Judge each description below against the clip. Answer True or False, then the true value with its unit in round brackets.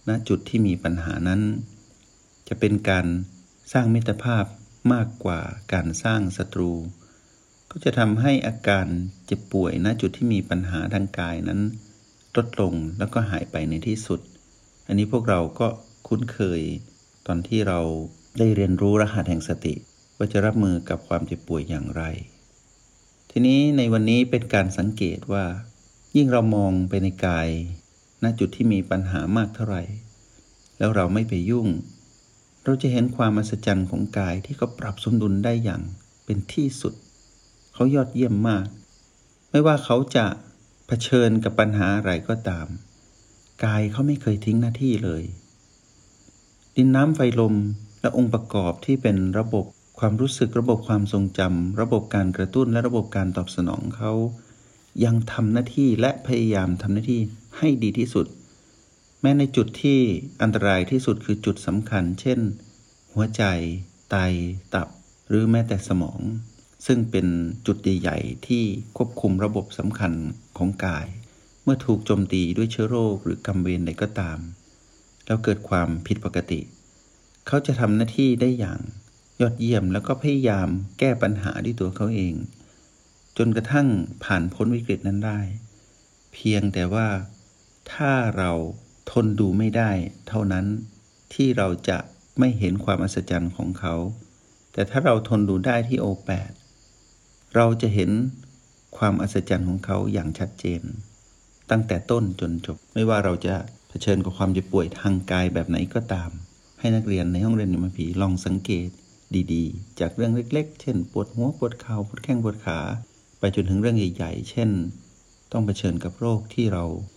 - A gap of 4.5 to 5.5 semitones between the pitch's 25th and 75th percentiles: False (3.7 semitones)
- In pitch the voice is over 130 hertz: False (105 Hz)